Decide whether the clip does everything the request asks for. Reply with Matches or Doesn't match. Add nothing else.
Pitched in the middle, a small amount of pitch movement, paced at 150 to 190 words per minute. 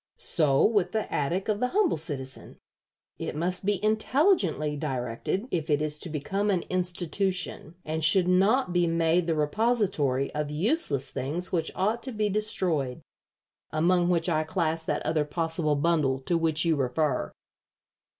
Doesn't match